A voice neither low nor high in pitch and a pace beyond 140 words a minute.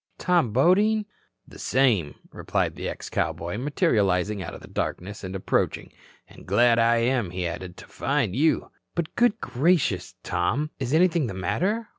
No: low, 120 Hz; average, 160 wpm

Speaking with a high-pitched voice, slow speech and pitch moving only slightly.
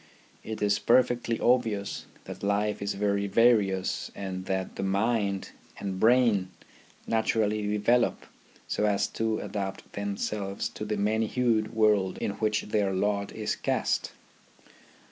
No: low, 105 Hz; slow, 130 wpm; narrow, 1.8 semitones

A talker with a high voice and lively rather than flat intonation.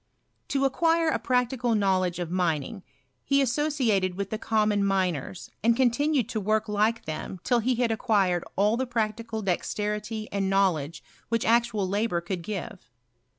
No: high, 215 Hz; average, 3.9 semitones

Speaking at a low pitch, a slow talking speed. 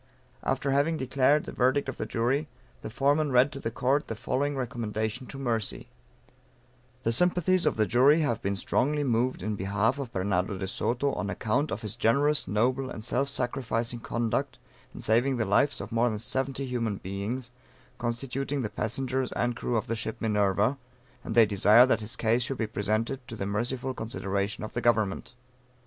No: low, 120 Hz; average, 185 wpm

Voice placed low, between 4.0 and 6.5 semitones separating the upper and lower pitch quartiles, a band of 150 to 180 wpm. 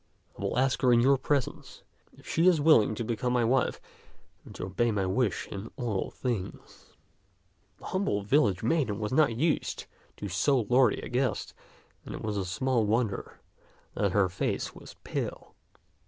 Yes: low, 120 Hz; average, 4.5 semitones; average, 170 wpm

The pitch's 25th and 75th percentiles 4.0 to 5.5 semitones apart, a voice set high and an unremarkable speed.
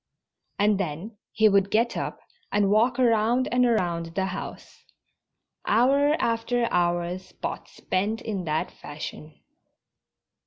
No: average, 4.7 semitones; high, 205 Hz; slow, 120 wpm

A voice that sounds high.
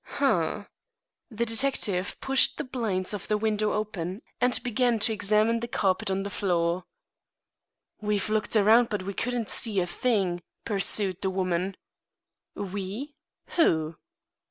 Yes: high, 210 Hz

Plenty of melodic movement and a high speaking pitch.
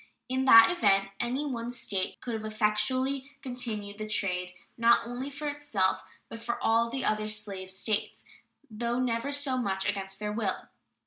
No: average, 3.7 semitones; high, 230 Hz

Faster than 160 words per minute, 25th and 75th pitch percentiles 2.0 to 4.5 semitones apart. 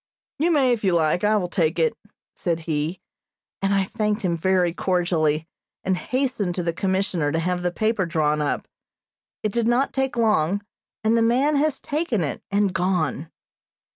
No: average, 175 wpm; average, 5.2 semitones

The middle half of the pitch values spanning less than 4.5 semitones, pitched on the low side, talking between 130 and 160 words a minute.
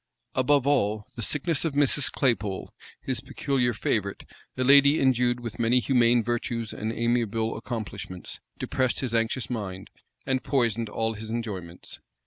Yes: average, 2.8 semitones; low, 120 Hz; average, 140 wpm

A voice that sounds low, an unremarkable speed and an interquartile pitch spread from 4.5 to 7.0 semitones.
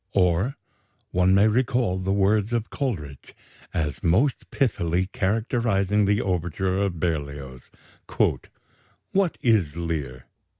No: very low, 95 Hz; slow, 110 wpm; average, 4.8 semitones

